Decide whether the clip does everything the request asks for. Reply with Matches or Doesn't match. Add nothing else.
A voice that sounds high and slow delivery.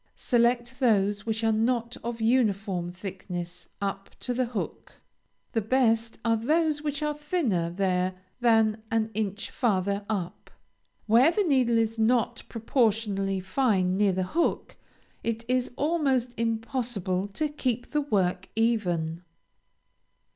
Matches